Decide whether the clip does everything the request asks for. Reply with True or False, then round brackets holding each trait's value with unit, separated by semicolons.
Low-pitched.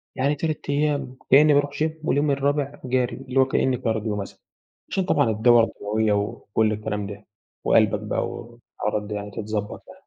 True (120 Hz)